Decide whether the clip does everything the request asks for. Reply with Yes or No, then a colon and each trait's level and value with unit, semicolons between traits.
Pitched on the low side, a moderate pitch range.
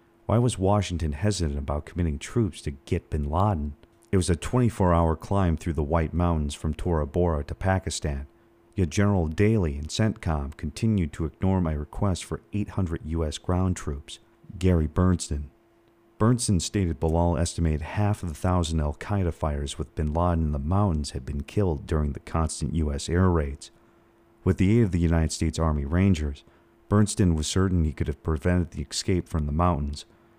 Yes: very low, 85 Hz; average, 4.1 semitones